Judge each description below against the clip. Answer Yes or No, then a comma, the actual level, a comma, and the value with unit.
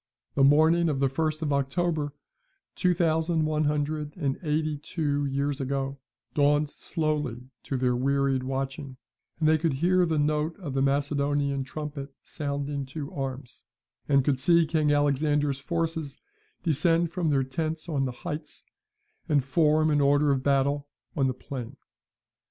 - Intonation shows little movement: Yes, narrow, 2.3 semitones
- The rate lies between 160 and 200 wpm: No, average, 150 wpm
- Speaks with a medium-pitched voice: Yes, medium, 145 Hz